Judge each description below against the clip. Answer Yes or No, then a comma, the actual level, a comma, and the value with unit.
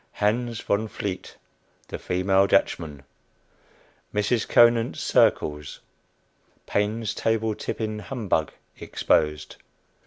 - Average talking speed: No, slow, 85 wpm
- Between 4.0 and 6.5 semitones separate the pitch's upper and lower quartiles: No, average, 3.6 semitones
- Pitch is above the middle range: No, low, 105 Hz